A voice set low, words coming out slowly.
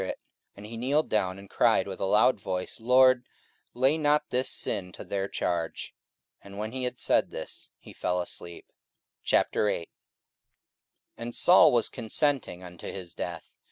No: low, 110 Hz; average, 160 wpm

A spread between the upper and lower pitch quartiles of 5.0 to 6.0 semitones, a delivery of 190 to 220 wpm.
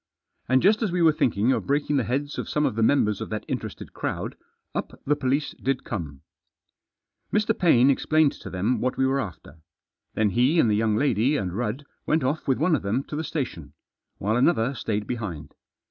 Yes: wide, 5.5 semitones; fast, 205 wpm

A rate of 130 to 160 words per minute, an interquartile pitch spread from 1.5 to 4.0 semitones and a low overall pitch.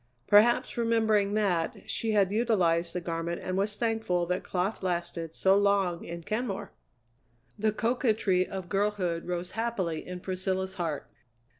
No: average, 140 wpm; average, 3.4 semitones; high, 190 Hz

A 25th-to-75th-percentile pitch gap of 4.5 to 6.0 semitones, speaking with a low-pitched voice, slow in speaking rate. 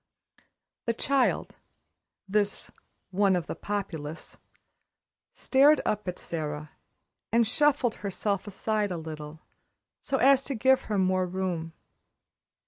No: average, 5.1 semitones; high, 200 Hz; slow, 115 wpm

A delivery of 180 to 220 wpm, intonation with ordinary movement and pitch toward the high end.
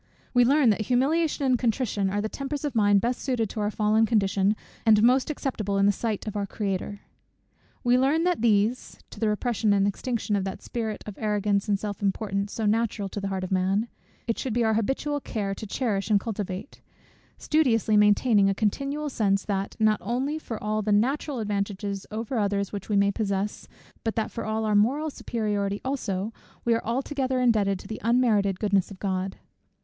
Yes: average, 195 wpm; average, 3.3 semitones; high, 215 Hz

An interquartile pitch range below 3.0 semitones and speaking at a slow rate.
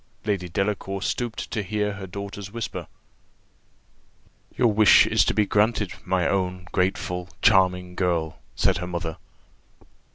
Yes: narrow, 2.5 semitones; slow, 120 wpm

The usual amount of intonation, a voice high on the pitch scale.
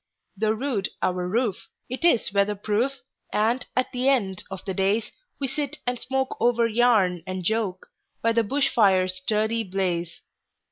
Yes: average, 4.5 semitones; high, 220 Hz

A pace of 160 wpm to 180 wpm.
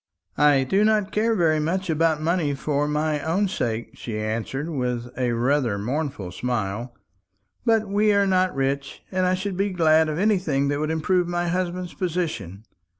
Yes: average, 170 wpm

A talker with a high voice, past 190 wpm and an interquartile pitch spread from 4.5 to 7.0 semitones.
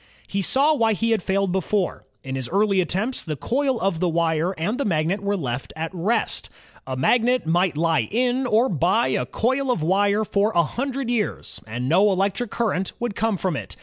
Yes: high, 195 Hz; average, 200 wpm; wide, 5.6 semitones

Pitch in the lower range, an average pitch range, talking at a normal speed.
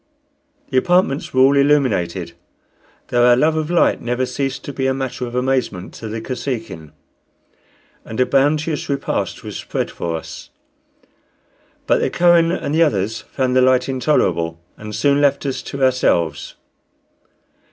Yes: low, 130 Hz; average, 4.0 semitones; average, 150 wpm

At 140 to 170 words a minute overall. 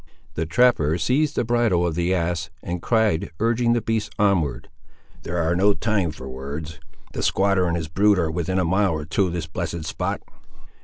No: average, 195 wpm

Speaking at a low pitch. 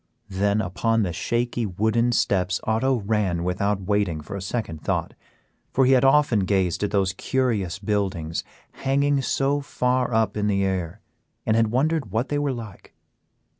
Yes: low, 105 Hz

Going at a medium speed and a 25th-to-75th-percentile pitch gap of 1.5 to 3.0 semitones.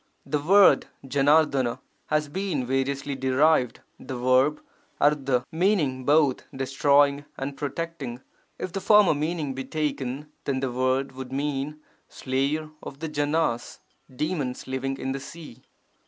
No: slow, 130 wpm; narrow, 2.6 semitones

